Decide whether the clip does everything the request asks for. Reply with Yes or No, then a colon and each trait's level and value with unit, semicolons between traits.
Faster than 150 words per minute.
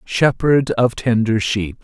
No: slow, 130 wpm